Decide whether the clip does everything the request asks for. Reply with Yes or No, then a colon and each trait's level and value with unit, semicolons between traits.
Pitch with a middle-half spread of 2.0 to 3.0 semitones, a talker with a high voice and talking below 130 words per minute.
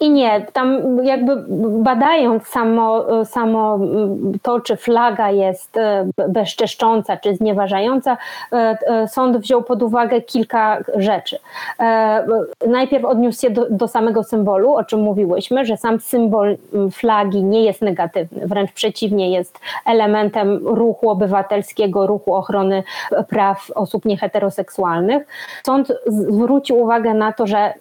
Yes: average, 2.7 semitones; high, 220 Hz; average, 115 wpm